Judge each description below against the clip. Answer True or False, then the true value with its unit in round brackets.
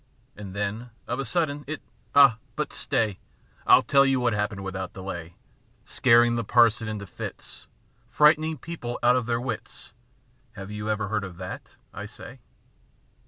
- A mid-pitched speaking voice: False (115 Hz)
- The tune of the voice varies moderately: True (4.0 semitones)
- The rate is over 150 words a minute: True (175 wpm)